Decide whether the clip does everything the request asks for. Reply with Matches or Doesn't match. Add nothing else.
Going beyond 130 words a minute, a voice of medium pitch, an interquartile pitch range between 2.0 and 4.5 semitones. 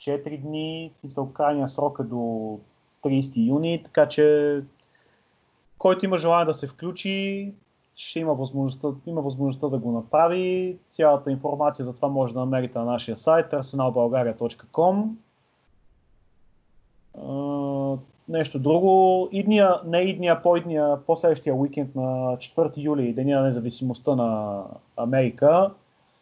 Doesn't match